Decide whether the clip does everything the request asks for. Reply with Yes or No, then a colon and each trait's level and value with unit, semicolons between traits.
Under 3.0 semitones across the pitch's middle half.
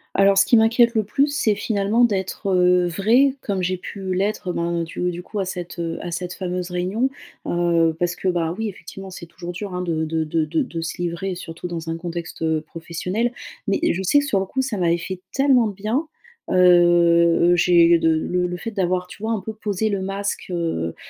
No: average, 3.3 semitones